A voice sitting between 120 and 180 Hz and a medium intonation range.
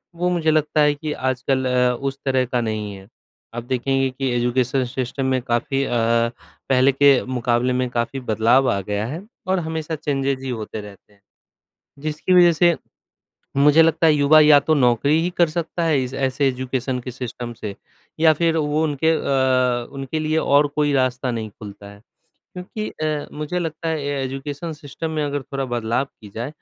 Yes: low, 135 Hz; average, 3.7 semitones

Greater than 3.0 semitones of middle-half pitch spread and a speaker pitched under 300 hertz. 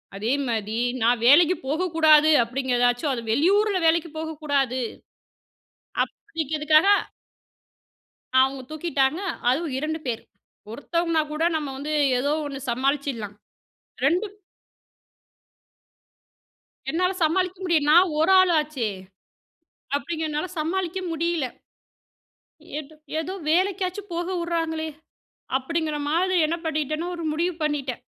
No: average, 3.7 semitones; very high, 310 Hz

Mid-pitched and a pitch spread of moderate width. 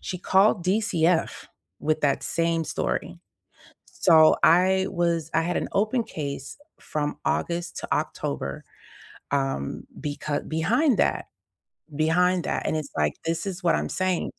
Yes: medium, 165 Hz; average, 3.1 semitones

